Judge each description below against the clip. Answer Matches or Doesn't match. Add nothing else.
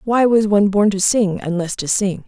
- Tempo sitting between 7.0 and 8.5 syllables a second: Doesn't match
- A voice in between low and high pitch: Doesn't match